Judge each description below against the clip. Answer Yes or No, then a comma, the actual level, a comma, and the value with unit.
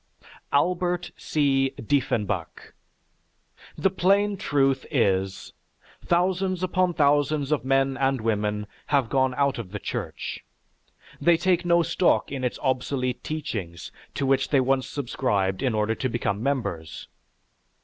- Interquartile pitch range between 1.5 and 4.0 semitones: No, average, 5.2 semitones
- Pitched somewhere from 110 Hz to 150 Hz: Yes, low, 135 Hz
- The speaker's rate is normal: No, slow, 130 wpm